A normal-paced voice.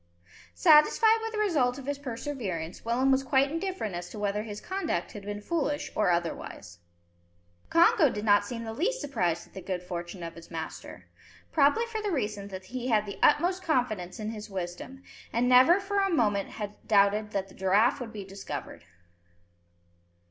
Yes: average, 180 wpm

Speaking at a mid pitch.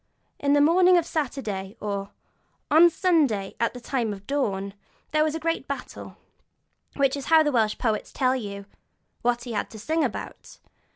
No: very high, 260 Hz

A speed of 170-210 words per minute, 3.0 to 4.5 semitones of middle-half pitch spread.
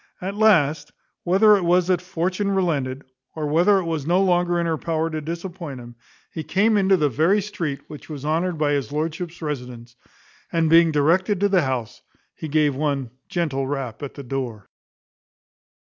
Yes: average, 175 wpm; average, 4.1 semitones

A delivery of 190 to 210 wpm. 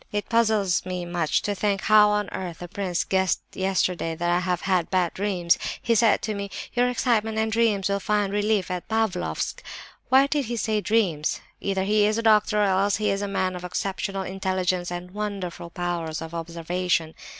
Yes: average, 195 wpm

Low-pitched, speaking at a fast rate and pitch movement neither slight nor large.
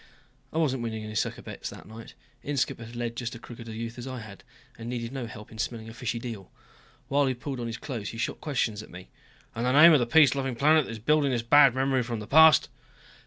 Yes: low, 120 Hz; fast, 255 wpm; average, 3.1 semitones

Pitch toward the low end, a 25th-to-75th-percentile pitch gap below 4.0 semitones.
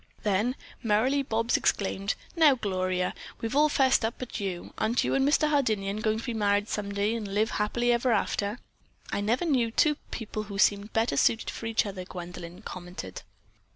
No: high, 215 Hz; average, 3.3 semitones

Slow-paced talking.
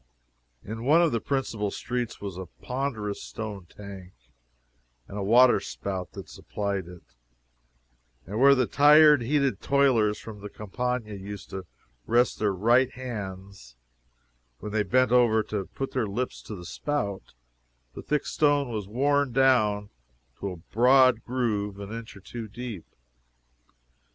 No: average, 145 wpm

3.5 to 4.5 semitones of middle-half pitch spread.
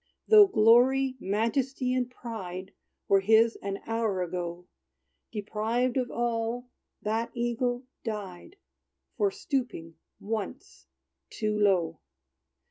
Yes: average, 3.8 semitones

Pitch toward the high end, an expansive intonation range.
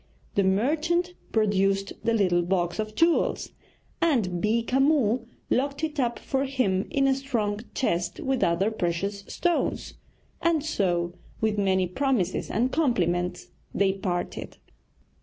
Yes: high, 215 Hz; wide, 6.3 semitones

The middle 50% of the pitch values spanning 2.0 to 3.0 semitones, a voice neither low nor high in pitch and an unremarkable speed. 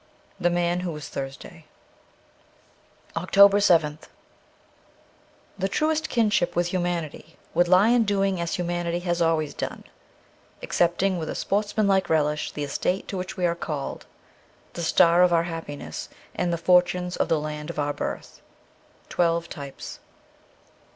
Yes: narrow, 2.4 semitones; medium, 175 Hz; average, 150 wpm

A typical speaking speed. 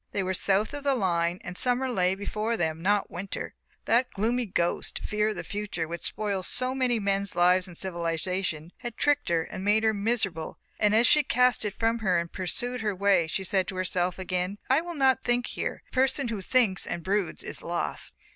No: fast, 210 wpm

